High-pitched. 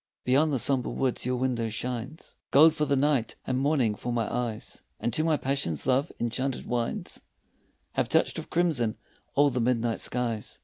No: low, 125 Hz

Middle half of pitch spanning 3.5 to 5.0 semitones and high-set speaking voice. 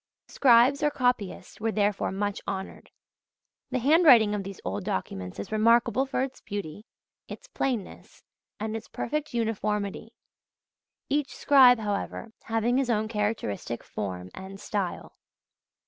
Yes: average, 4.0 semitones; high, 220 Hz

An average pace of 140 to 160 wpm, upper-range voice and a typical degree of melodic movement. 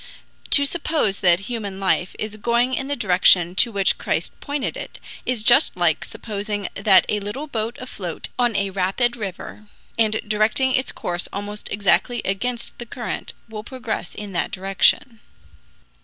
Yes: average, 155 wpm; high, 210 Hz; average, 3.7 semitones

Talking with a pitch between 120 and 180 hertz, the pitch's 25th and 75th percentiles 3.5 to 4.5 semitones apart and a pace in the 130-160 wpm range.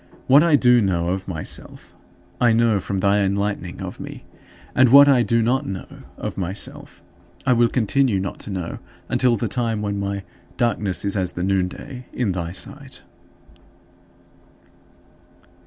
No: low, 105 Hz; average, 4.2 semitones; average, 155 wpm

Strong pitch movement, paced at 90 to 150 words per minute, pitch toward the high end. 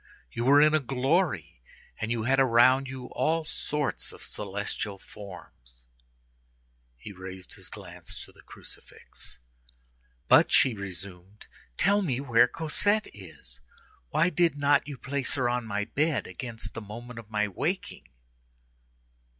No: wide, 5.8 semitones; average, 140 wpm; low, 120 Hz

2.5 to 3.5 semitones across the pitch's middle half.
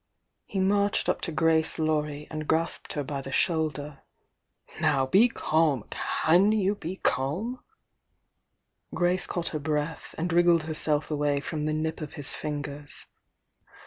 Yes: average, 2.9 semitones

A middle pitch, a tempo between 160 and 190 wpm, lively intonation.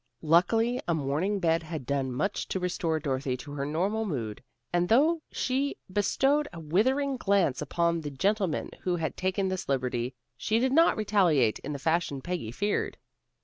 Yes: medium, 175 Hz; average, 175 wpm; wide, 6.3 semitones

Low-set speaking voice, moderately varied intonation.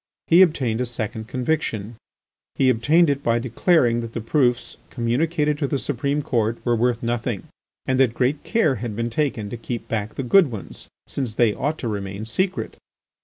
Yes: low, 120 Hz; average, 3.9 semitones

